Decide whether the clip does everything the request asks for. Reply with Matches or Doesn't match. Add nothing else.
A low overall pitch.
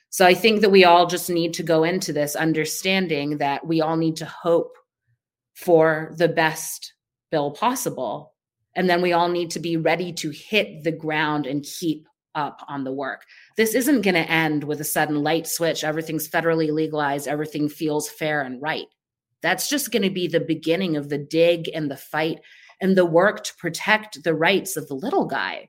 Doesn't match